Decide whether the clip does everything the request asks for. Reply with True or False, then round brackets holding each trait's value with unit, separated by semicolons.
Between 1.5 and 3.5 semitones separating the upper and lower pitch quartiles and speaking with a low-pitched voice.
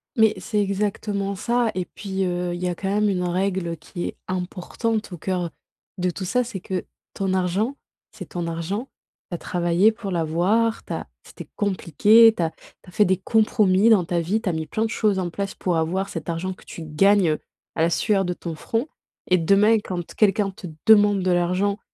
False (3.0 semitones; 190 Hz)